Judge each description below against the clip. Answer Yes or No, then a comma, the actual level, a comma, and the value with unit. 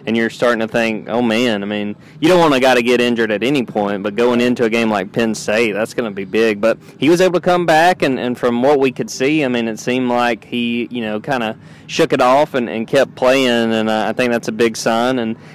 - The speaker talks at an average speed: No, fast, 280 wpm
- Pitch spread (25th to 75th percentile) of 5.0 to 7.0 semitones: No, average, 2.7 semitones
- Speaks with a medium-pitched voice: No, low, 120 Hz